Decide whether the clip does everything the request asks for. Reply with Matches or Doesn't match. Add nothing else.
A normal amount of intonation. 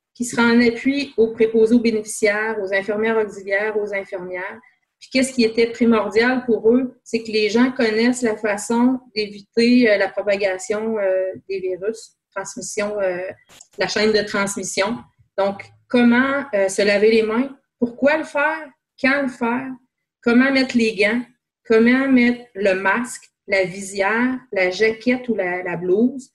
Matches